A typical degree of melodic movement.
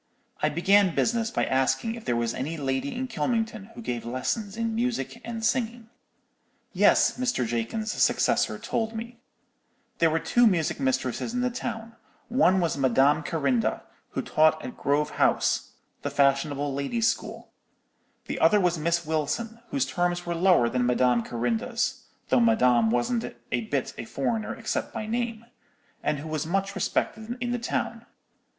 No: wide, 8.8 semitones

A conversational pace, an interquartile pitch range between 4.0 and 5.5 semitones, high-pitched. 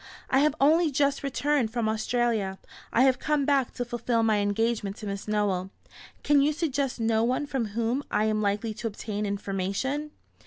Yes: average, 180 wpm; average, 4.6 semitones; high, 235 Hz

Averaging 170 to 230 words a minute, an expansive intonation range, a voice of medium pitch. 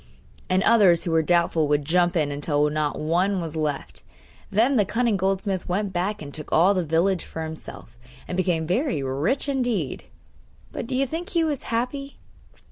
Yes: average, 180 wpm; wide, 6.2 semitones; medium, 180 Hz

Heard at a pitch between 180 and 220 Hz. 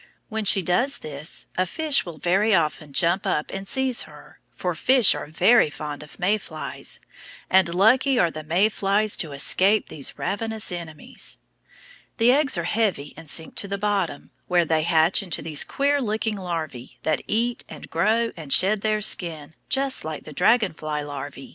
Yes: medium, 185 Hz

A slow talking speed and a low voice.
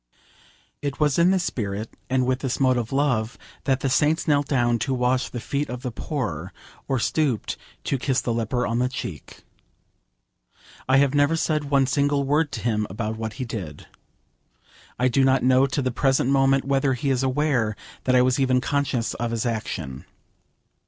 No: average, 185 wpm; low, 130 Hz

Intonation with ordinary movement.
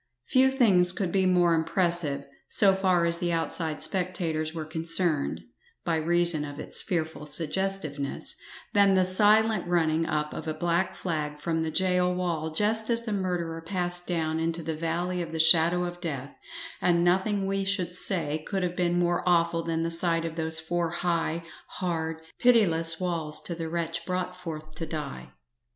No: narrow, 2.1 semitones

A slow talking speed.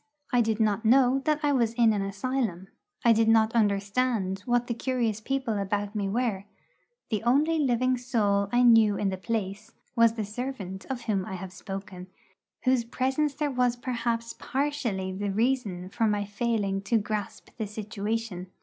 No: average, 170 wpm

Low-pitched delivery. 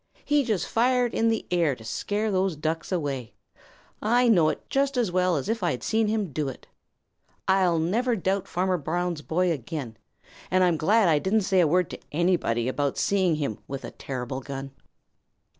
No: medium, 180 Hz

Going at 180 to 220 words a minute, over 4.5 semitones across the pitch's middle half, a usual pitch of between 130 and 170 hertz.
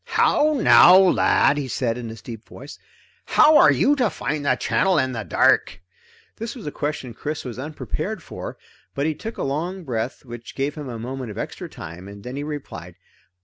Yes: average, 195 wpm; average, 5.0 semitones; low, 135 Hz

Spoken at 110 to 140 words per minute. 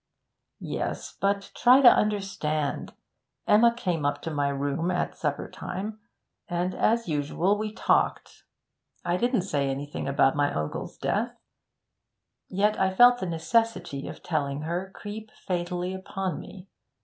Yes: slow, 135 wpm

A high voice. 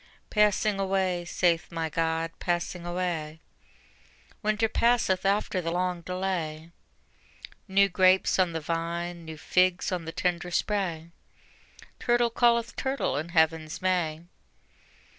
No: medium, 180 Hz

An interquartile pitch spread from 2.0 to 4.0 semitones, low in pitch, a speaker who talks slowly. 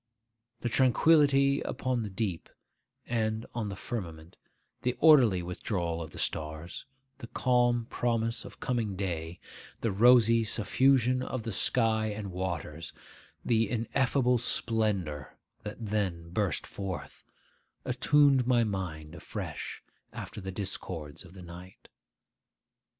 No: average, 5.1 semitones; low, 110 Hz; slow, 120 wpm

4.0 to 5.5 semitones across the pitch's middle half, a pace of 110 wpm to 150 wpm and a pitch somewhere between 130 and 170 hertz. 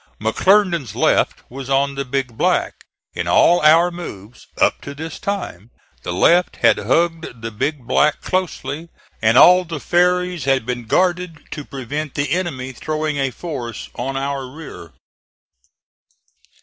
Yes: average, 5.1 semitones; average, 145 wpm; medium, 140 Hz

